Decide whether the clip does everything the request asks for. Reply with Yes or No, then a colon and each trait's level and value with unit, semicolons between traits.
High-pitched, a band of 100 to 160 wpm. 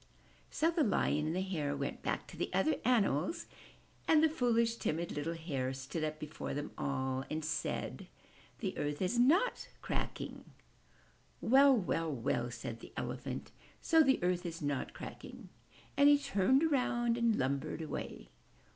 No: medium, 175 Hz; average, 155 wpm